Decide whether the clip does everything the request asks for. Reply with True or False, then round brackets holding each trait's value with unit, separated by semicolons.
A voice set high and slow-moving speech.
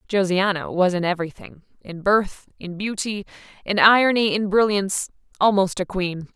True (195 Hz; 125 wpm)